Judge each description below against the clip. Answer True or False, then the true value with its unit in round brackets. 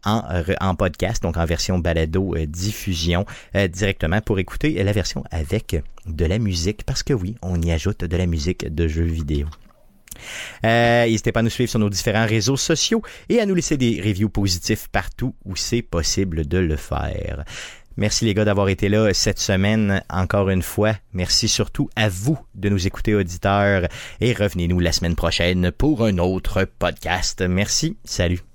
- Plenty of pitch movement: False (3.8 semitones)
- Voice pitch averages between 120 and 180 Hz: False (100 Hz)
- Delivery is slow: False (180 wpm)